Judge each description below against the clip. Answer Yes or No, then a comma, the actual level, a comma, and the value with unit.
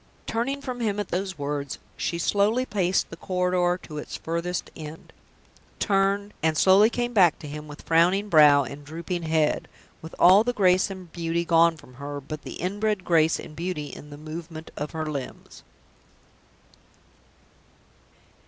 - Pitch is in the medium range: Yes, medium, 170 Hz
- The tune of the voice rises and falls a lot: No, average, 4.1 semitones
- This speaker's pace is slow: No, average, 160 wpm